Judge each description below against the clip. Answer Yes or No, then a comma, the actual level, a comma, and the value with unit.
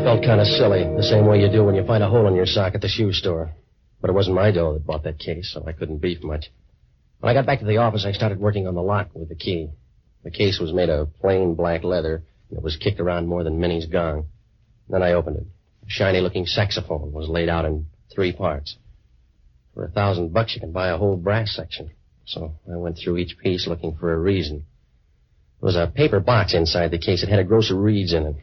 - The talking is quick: Yes, fast, 250 wpm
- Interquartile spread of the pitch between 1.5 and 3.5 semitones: No, average, 4.1 semitones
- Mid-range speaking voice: No, very low, 90 Hz